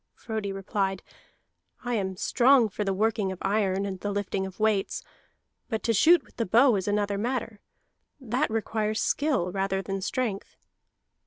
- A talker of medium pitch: No, high, 205 Hz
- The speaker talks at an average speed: Yes, average, 160 wpm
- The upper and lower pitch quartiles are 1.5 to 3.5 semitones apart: Yes, average, 2.8 semitones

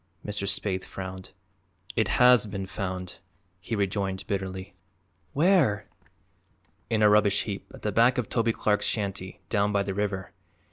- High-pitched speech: No, low, 100 Hz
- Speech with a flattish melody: Yes, narrow, 2.1 semitones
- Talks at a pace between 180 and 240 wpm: No, average, 145 wpm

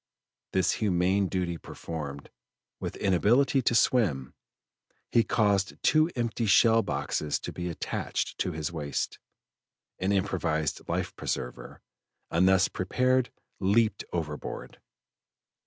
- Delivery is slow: Yes, slow, 110 wpm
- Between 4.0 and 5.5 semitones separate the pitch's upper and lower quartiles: Yes, average, 5.2 semitones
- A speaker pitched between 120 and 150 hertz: No, very low, 95 Hz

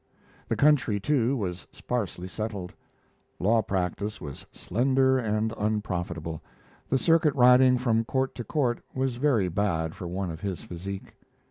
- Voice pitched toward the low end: Yes, low, 110 Hz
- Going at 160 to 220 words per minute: No, average, 140 wpm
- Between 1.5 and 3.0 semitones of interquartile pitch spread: No, wide, 5.6 semitones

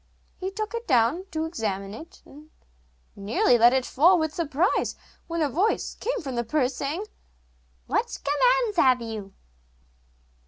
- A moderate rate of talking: Yes, average, 150 wpm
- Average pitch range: No, wide, 7.3 semitones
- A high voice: Yes, very high, 300 Hz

